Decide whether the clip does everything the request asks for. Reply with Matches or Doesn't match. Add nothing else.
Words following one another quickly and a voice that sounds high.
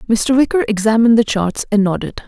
Doesn't match